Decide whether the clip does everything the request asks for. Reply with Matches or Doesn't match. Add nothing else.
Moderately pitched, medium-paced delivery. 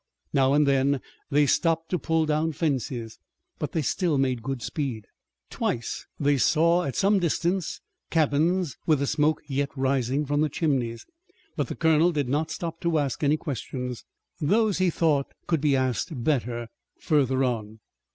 Matches